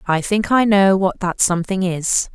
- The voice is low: No, high, 190 Hz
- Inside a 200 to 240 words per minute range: Yes, fast, 205 wpm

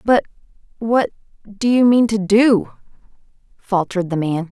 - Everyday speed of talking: No, slow, 105 wpm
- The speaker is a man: No, female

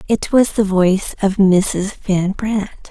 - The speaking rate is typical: Yes, average, 165 wpm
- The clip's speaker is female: Yes, female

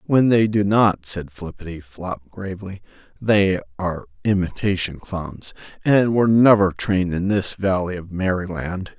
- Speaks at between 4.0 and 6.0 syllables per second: Yes, 4.5 syllables/s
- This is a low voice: Yes, very low, 95 Hz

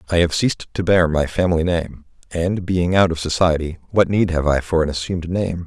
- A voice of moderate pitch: No, very low, 85 Hz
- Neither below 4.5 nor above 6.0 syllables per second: Yes, 5.6 syllables/s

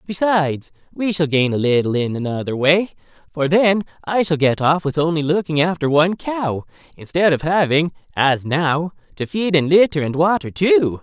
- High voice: No, medium, 160 Hz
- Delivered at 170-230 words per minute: Yes, average, 180 wpm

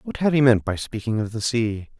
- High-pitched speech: No, low, 120 Hz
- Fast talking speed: Yes, fast, 270 wpm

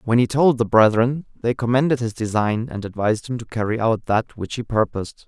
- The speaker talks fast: Yes, fast, 215 wpm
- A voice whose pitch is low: Yes, low, 115 Hz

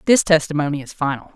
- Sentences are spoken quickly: No, average, 180 wpm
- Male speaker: No, female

